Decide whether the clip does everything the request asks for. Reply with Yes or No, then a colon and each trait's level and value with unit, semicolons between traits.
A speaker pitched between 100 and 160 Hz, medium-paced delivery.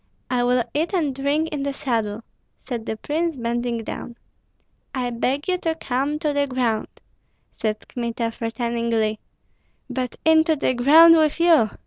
No: very high, 255 Hz; average, 150 wpm